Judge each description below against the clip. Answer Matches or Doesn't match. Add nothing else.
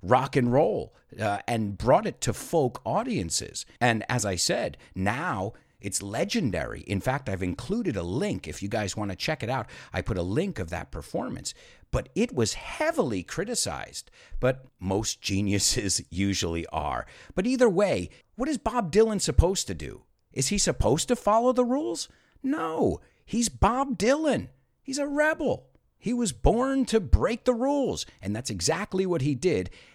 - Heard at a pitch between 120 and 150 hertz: Matches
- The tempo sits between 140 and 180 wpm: Matches